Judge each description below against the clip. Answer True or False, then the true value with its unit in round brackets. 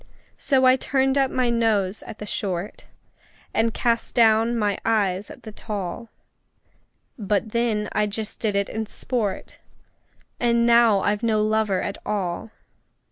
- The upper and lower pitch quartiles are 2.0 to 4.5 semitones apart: True (2.4 semitones)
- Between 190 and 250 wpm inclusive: False (145 wpm)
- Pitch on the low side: False (220 Hz)